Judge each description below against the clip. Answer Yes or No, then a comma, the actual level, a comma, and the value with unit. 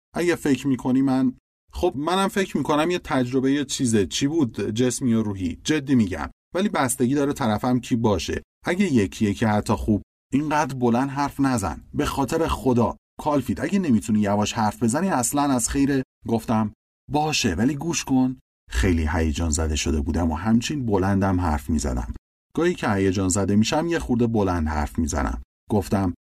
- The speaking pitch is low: Yes, low, 120 Hz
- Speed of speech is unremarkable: No, fast, 165 wpm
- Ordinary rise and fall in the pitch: No, wide, 6.1 semitones